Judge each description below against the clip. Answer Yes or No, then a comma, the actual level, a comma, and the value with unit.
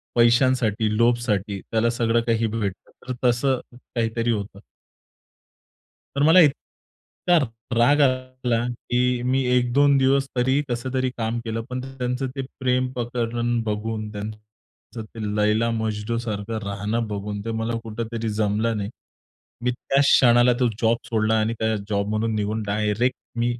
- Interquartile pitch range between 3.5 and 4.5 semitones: No, narrow, 2.6 semitones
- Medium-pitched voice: No, low, 115 Hz